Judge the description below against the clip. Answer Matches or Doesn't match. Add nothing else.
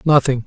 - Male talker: Matches